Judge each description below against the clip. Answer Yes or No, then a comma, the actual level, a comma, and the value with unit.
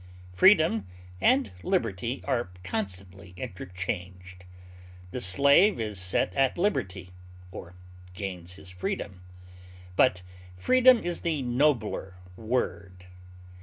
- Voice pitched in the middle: No, low, 100 Hz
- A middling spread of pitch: No, wide, 6.4 semitones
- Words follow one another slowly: Yes, slow, 95 wpm